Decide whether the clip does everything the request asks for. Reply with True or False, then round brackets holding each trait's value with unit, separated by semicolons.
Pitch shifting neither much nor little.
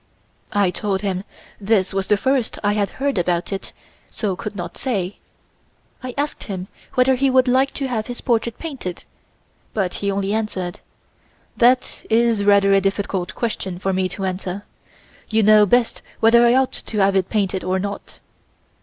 True (3.7 semitones)